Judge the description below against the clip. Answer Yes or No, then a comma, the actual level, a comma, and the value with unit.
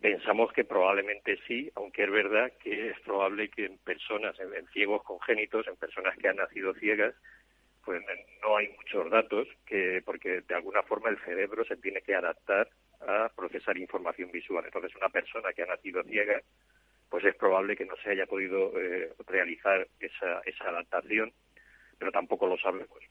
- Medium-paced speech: Yes, average, 170 wpm